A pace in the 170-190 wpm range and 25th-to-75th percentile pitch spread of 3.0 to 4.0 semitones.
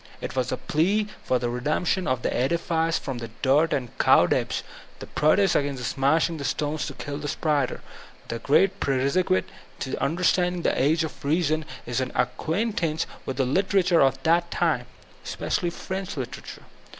No: average, 175 wpm; average, 4.5 semitones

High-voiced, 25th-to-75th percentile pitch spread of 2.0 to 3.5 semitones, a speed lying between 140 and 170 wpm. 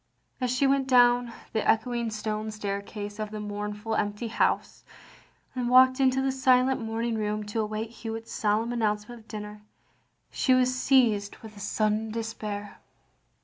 Yes: high, 225 Hz; average, 2.8 semitones; average, 150 wpm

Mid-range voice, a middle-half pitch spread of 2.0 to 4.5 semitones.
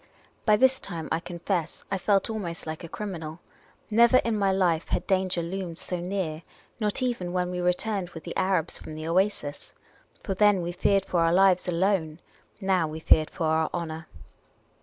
Yes: medium, 180 Hz; average, 2.9 semitones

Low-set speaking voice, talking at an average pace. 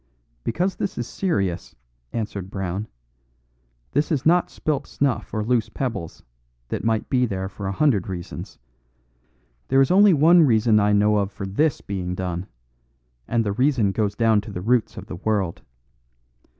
Yes: low, 110 Hz; average, 165 wpm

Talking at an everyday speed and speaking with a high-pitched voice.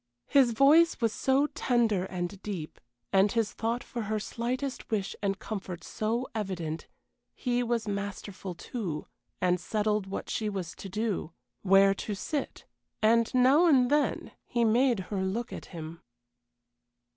Yes: average, 145 wpm; high, 215 Hz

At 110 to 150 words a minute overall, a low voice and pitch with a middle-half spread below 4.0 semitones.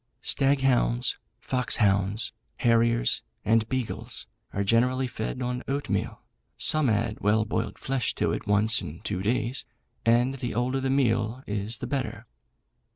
Yes: average, 145 wpm; low, 120 Hz; average, 3.0 semitones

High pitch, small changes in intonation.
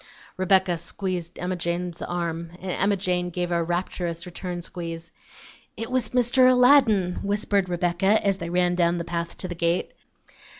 No: medium, 180 Hz; narrow, 2.3 semitones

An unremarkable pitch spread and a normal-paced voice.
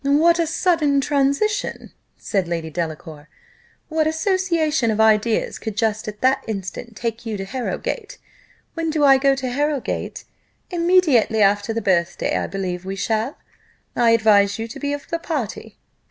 No: wide, 6.8 semitones; average, 155 wpm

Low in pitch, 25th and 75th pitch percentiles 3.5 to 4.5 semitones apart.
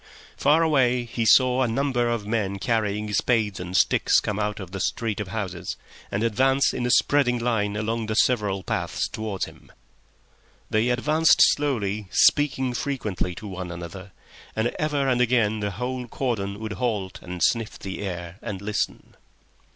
Yes: low, 110 Hz; average, 3.8 semitones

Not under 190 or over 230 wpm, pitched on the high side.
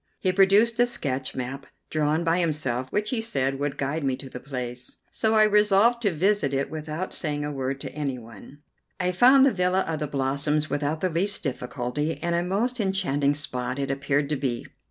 No: average, 195 wpm; medium, 150 Hz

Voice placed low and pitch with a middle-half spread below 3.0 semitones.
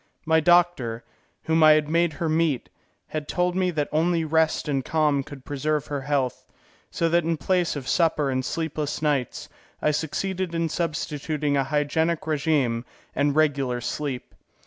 No: medium, 155 Hz; narrow, 2.5 semitones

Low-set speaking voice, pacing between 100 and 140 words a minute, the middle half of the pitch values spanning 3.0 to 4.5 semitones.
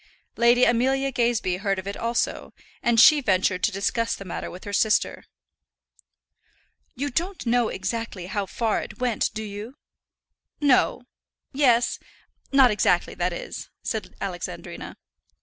No: high, 230 Hz; slow, 135 wpm; average, 3.9 semitones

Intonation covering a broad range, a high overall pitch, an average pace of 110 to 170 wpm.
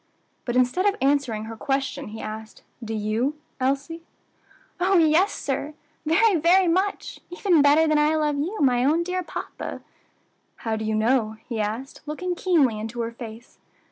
Yes: wide, 6.4 semitones; very high, 280 Hz; average, 165 wpm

